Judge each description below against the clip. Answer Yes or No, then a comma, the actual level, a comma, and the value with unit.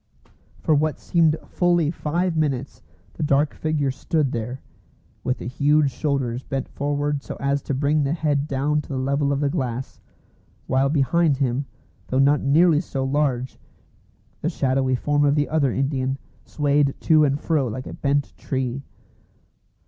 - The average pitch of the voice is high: No, medium, 140 Hz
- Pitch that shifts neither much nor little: No, narrow, 2.1 semitones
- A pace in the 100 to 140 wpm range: No, average, 160 wpm